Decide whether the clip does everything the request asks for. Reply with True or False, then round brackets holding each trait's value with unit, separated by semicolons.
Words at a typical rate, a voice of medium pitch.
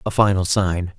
False (185 wpm; 95 Hz)